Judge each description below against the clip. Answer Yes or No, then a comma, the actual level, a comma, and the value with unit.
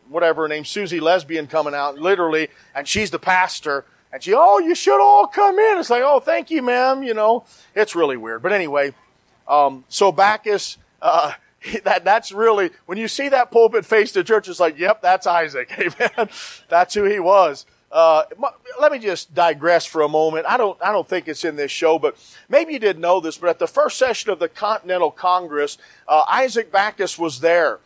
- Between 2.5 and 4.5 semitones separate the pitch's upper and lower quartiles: No, wide, 5.6 semitones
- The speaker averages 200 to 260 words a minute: Yes, fast, 205 wpm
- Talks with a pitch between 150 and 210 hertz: Yes, medium, 185 Hz